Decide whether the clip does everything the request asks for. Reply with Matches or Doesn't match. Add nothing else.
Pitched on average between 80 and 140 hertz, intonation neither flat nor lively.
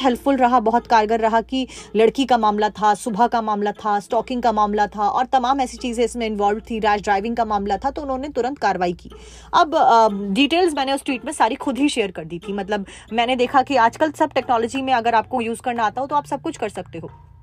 Doesn't match